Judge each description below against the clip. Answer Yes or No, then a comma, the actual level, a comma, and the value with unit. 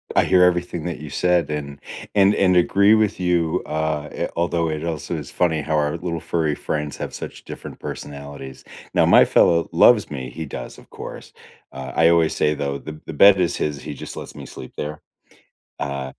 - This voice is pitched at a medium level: No, very low, 80 Hz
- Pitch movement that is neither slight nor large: Yes, average, 3.2 semitones